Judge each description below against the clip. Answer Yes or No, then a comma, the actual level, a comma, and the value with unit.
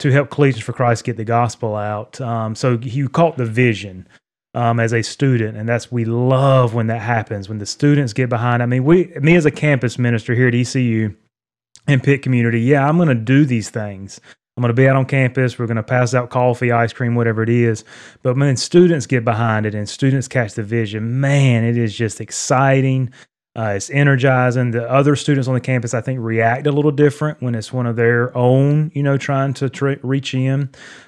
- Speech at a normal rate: No, fast, 220 wpm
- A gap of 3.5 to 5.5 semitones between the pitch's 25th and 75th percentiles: No, average, 2.8 semitones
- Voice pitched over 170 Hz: No, low, 125 Hz